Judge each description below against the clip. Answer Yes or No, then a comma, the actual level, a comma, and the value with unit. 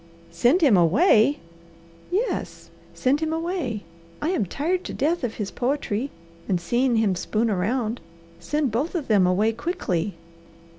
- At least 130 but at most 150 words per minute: Yes, average, 145 wpm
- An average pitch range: No, wide, 6.7 semitones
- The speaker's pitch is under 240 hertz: No, high, 245 Hz